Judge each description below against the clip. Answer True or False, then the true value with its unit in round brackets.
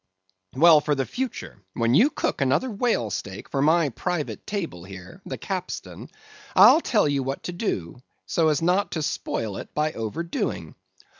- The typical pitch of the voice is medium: True (150 Hz)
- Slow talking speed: False (165 wpm)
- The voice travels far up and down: True (6.7 semitones)